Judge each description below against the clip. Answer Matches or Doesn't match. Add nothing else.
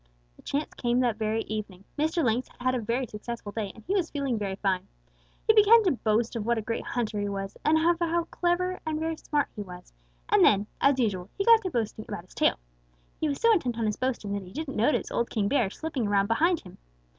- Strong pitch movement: Matches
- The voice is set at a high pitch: Matches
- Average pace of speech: Doesn't match